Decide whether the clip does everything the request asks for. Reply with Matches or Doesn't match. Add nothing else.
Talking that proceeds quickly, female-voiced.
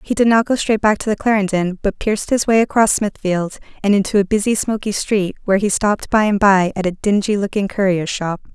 Matches